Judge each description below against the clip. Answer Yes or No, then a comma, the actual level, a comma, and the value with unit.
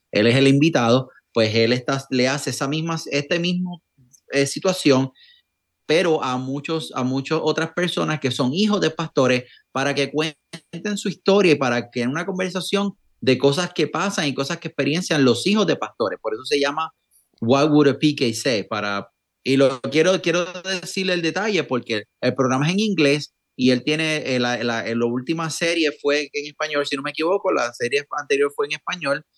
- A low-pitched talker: No, medium, 150 Hz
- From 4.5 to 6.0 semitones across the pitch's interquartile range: Yes, average, 5.1 semitones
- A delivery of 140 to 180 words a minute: No, average, 195 wpm